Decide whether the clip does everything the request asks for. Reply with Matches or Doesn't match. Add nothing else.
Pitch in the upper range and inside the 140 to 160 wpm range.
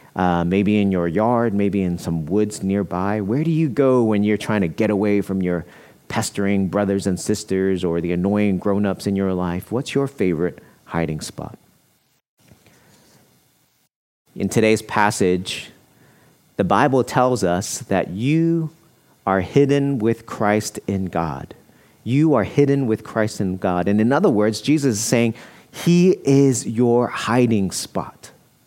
Doesn't match